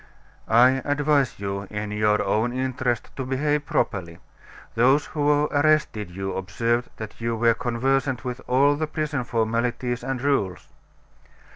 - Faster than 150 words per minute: No, slow, 135 wpm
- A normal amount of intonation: Yes, average, 4.2 semitones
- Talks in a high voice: No, low, 125 Hz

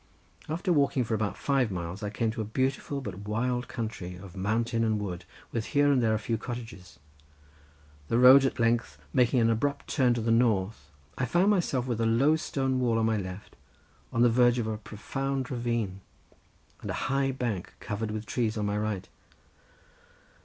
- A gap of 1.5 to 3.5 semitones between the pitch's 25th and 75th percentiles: Yes, average, 3.2 semitones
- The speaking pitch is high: No, low, 115 Hz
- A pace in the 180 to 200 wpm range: Yes, average, 190 wpm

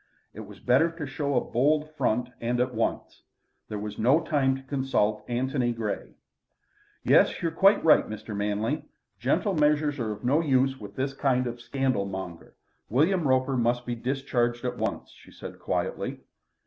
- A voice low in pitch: Yes, low, 130 Hz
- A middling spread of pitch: Yes, average, 3.3 semitones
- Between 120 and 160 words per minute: No, average, 170 wpm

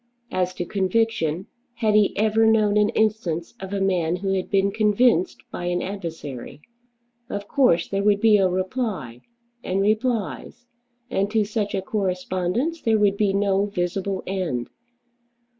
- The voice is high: Yes, high, 200 Hz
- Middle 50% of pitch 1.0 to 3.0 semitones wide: Yes, average, 2.7 semitones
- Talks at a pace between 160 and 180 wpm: No, average, 150 wpm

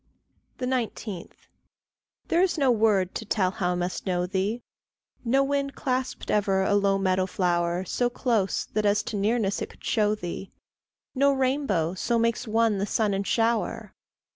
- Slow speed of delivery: No, average, 165 wpm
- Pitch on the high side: Yes, high, 210 Hz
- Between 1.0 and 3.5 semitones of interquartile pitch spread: No, average, 4.2 semitones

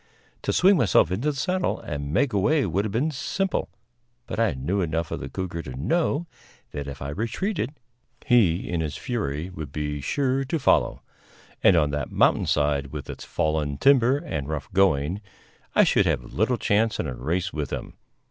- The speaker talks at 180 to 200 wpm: Yes, average, 185 wpm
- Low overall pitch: Yes, very low, 90 Hz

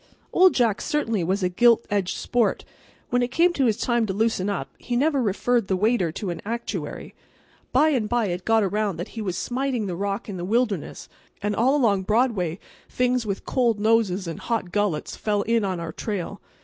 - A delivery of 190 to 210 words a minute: Yes, average, 200 wpm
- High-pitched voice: Yes, high, 215 Hz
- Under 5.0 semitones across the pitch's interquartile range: Yes, average, 3.9 semitones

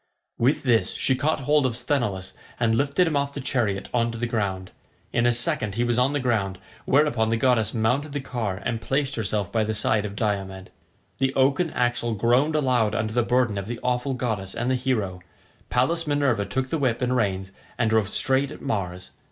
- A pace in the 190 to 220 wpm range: Yes, fast, 205 wpm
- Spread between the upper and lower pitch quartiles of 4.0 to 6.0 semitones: No, average, 3.5 semitones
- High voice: No, low, 120 Hz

